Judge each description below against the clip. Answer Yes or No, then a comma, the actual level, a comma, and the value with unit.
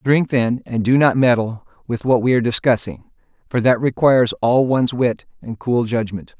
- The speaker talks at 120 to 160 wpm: No, average, 190 wpm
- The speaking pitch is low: Yes, low, 120 Hz